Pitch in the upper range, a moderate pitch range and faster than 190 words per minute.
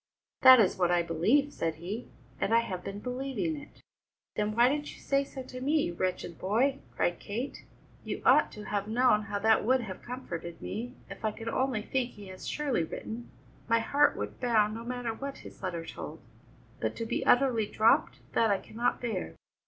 Yes: high, 225 Hz; average, 4.5 semitones; average, 200 wpm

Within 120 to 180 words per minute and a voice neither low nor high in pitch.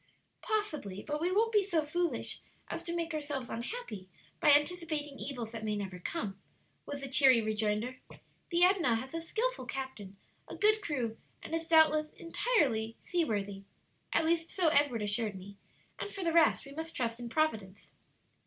No: average, 170 wpm; very high, 290 Hz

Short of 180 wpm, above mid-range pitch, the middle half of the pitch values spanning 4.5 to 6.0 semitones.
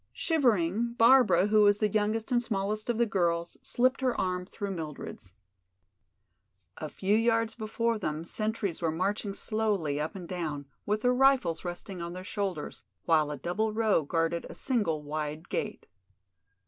Yes: average, 160 wpm; high, 200 Hz; average, 5.0 semitones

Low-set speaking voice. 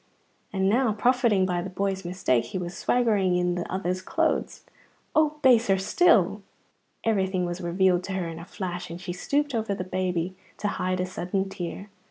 No: high, 190 Hz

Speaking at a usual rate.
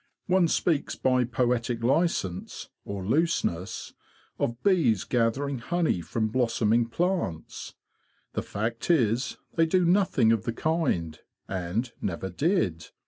No: slow, 125 wpm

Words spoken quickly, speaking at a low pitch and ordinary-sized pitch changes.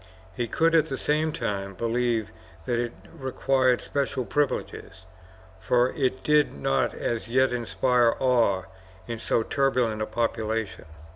No: slow, 135 wpm; low, 120 Hz; average, 3.0 semitones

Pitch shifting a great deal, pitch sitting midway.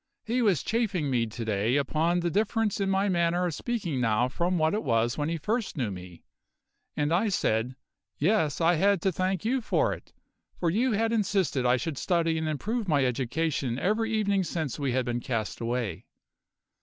Yes: wide, 7.8 semitones; medium, 165 Hz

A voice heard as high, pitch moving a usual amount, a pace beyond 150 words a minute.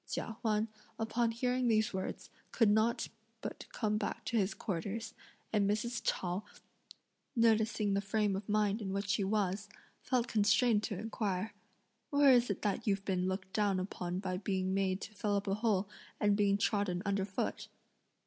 No: high, 205 Hz; narrow, 2.3 semitones; average, 170 wpm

